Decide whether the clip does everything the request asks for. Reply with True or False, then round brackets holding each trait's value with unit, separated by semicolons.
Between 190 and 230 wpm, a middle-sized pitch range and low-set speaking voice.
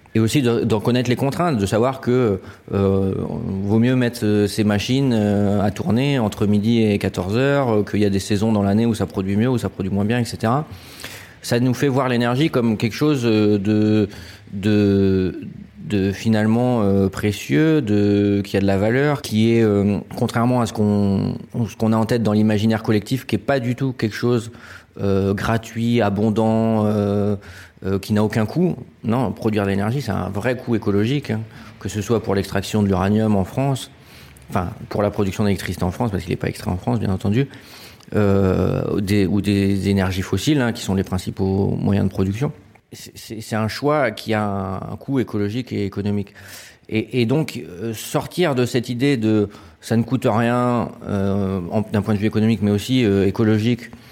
True (200 wpm; 3.1 semitones; 110 Hz)